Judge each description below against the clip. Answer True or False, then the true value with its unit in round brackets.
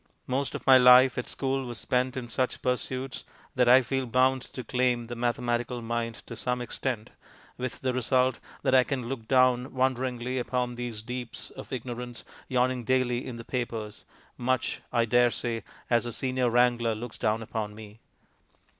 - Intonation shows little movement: True (1.5 semitones)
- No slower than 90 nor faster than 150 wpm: False (170 wpm)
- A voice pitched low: True (125 Hz)